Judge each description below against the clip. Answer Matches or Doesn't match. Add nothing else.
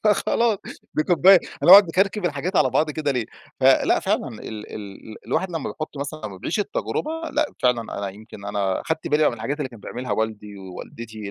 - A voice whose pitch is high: Doesn't match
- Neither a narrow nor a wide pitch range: Doesn't match